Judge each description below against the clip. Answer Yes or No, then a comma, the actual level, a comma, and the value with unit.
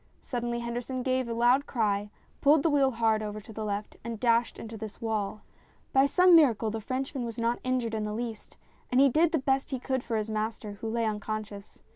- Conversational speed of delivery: No, fast, 215 wpm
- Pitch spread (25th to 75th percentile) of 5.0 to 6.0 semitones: No, average, 3.1 semitones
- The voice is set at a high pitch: Yes, high, 235 Hz